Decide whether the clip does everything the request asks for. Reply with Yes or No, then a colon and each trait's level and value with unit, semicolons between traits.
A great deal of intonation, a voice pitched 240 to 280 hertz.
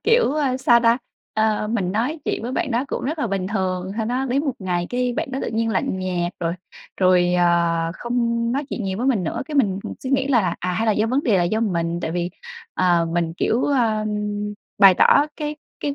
No: wide, 5.8 semitones; high, 220 Hz